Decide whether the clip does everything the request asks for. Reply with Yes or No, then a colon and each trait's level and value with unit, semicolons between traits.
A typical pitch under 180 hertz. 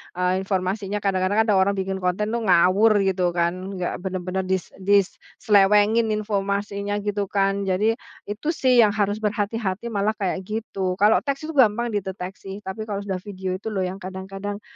No: high, 200 Hz